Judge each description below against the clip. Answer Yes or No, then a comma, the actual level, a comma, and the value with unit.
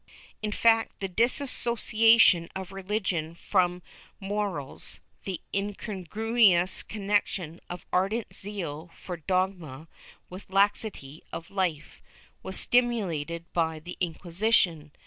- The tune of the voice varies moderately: Yes, average, 3.8 semitones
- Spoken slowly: Yes, slow, 110 wpm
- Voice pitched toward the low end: No, high, 190 Hz